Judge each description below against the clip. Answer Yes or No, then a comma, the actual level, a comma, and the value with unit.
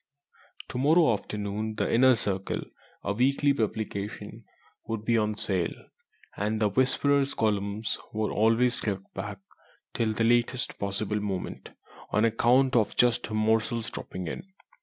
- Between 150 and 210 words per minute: No, average, 140 wpm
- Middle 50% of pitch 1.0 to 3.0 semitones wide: Yes, narrow, 2.6 semitones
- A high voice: No, low, 110 Hz